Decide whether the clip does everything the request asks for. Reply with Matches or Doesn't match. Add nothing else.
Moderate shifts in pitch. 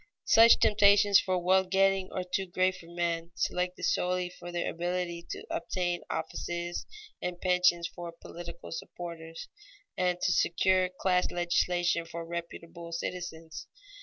Doesn't match